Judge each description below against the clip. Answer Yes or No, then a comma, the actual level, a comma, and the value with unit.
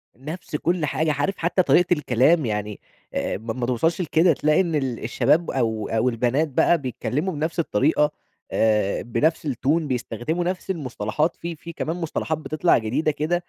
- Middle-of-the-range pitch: Yes, medium, 150 Hz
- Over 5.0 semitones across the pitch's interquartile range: Yes, wide, 5.4 semitones